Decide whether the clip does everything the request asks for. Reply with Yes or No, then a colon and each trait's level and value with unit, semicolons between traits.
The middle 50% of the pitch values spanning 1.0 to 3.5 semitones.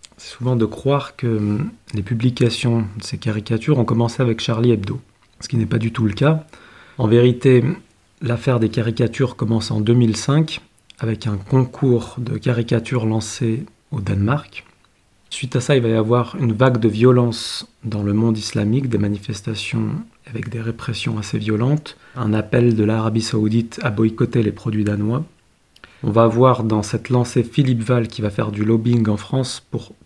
Yes: narrow, 2.4 semitones